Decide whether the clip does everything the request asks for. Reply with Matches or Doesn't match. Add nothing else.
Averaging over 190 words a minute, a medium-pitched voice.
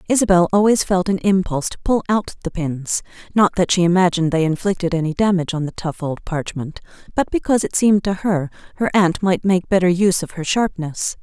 Matches